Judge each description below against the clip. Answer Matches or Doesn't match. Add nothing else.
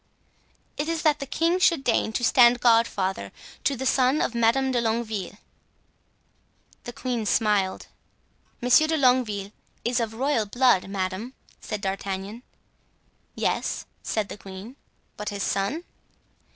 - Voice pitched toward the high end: Matches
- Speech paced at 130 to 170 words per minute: Matches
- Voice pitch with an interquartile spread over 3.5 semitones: Matches